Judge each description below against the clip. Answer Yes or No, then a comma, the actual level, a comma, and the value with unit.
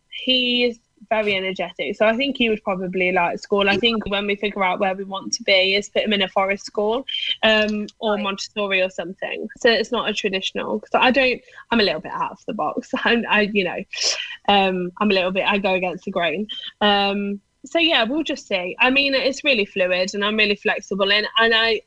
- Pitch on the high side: Yes, high, 205 Hz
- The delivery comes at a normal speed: No, fast, 230 wpm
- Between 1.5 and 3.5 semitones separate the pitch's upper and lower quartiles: Yes, average, 3.2 semitones